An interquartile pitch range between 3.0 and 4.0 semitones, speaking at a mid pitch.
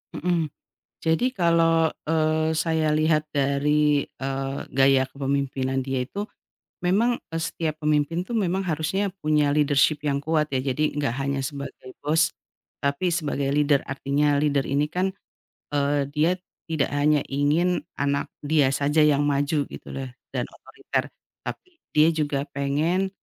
No: narrow, 2.5 semitones; medium, 150 Hz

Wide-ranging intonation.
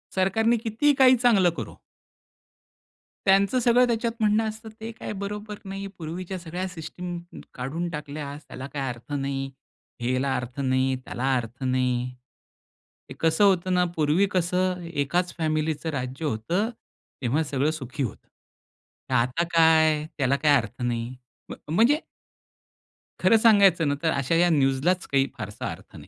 Yes: wide, 6.1 semitones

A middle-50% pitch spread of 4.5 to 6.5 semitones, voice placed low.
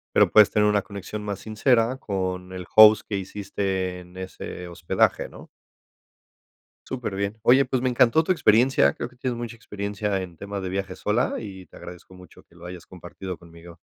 No: average, 3.3 semitones; low, 100 Hz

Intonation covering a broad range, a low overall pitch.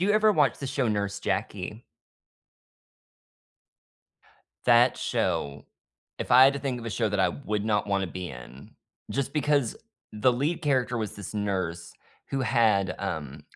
Yes: wide, 5.8 semitones; low, 105 Hz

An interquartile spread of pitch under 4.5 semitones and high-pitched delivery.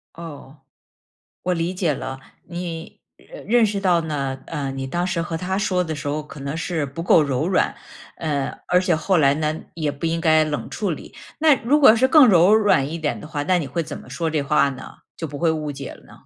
No: average, 3.8 semitones; medium, 160 Hz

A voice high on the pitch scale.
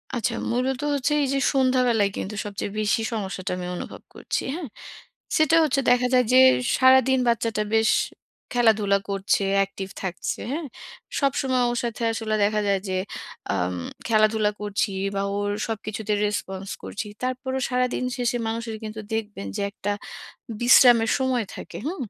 Yes: high, 225 Hz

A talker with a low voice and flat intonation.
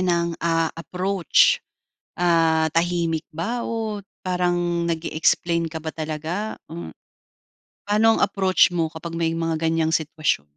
No: medium, 170 Hz; narrow, 1.8 semitones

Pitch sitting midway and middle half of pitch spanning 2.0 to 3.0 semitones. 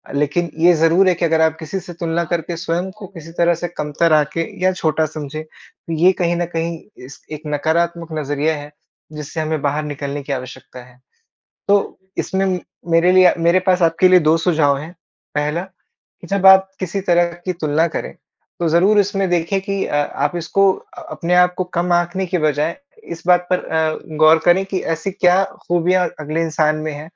Yes: medium, 170 Hz; narrow, 2.6 semitones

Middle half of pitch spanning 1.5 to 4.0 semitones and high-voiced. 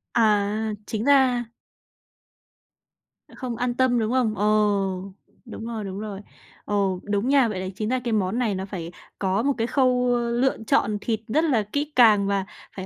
Yes: average, 3.4 semitones; high, 225 Hz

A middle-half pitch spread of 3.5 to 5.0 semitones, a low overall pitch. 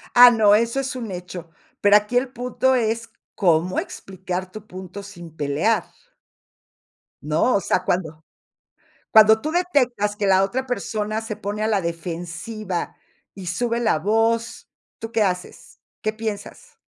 No: average, 4.0 semitones; high, 210 Hz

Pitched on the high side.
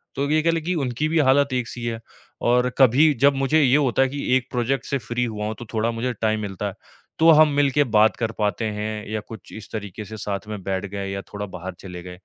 No: low, 120 Hz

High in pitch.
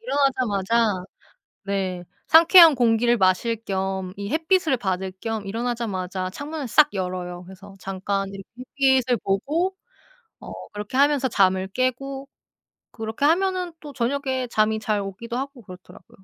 Yes: high, 225 Hz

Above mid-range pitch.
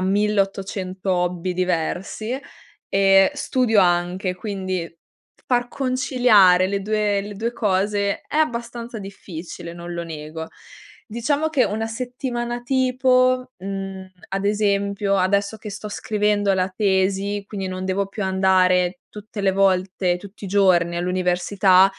Yes: high, 195 Hz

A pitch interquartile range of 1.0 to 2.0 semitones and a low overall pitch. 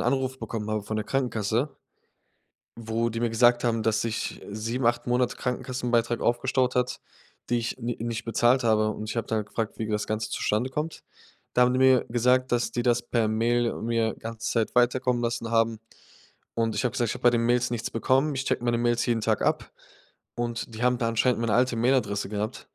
Yes: narrow, 1.7 semitones; low, 120 Hz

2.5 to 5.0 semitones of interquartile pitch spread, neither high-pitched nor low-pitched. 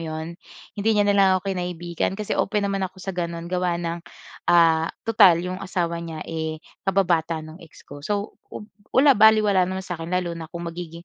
Yes: average, 2.8 semitones; medium, 175 Hz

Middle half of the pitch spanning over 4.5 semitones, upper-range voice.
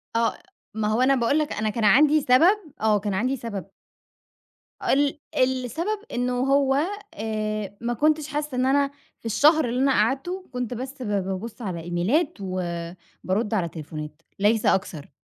Yes: average, 5.2 semitones; high, 235 Hz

